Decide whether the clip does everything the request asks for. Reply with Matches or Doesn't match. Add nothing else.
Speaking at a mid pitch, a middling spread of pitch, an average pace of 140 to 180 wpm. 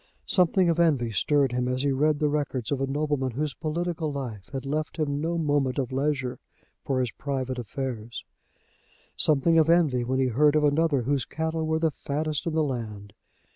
Doesn't match